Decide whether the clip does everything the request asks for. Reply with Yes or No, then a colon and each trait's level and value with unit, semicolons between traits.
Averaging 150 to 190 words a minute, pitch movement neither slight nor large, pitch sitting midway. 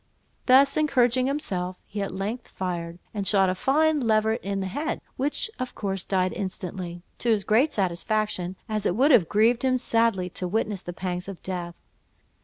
No: average, 180 wpm; average, 5.0 semitones; high, 205 Hz